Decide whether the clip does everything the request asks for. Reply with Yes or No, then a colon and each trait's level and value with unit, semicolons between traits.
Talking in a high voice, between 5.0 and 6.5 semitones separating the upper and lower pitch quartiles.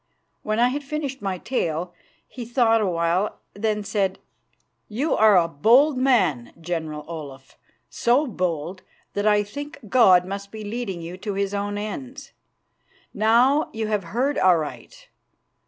Yes: high, 205 Hz; wide, 5.4 semitones